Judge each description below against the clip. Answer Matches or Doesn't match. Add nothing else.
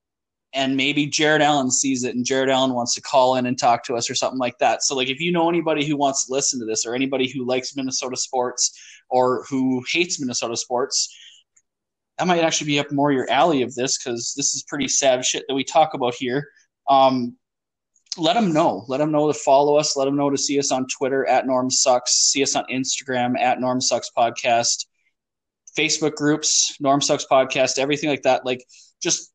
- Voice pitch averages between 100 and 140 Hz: Matches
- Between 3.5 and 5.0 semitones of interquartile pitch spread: Doesn't match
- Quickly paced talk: Matches